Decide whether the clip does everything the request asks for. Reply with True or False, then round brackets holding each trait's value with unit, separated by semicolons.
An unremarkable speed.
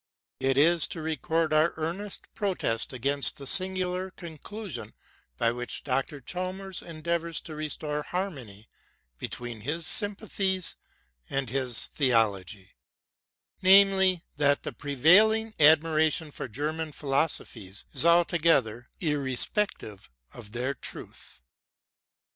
False (115 wpm)